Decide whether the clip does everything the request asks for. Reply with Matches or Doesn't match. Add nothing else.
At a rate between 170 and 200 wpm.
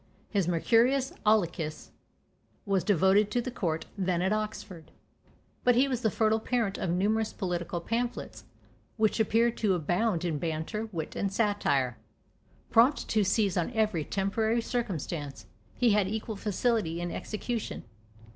Doesn't match